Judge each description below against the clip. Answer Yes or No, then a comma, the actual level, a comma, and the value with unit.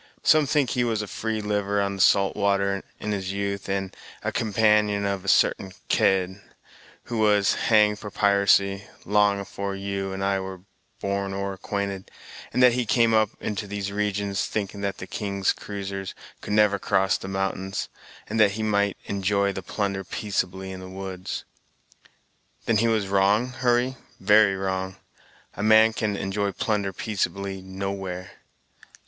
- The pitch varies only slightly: Yes, narrow, 1.5 semitones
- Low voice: Yes, low, 100 Hz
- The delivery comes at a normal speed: Yes, average, 160 wpm